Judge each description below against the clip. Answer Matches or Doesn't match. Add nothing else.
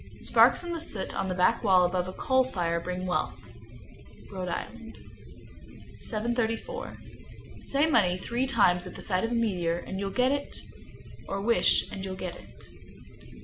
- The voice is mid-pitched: Doesn't match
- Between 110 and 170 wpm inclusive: Matches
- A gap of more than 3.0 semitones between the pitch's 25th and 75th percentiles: Matches